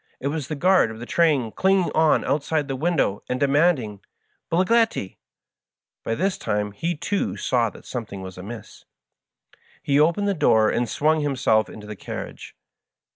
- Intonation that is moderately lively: No, wide, 7.2 semitones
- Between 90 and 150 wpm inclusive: No, average, 160 wpm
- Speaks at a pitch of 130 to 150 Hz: Yes, medium, 140 Hz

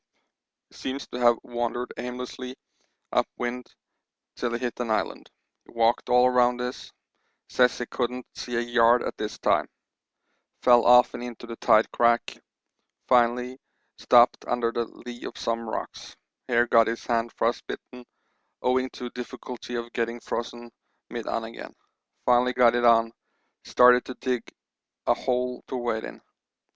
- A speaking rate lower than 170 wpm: Yes, average, 150 wpm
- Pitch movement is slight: Yes, narrow, 1.0 semitones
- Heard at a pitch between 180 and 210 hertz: No, low, 120 Hz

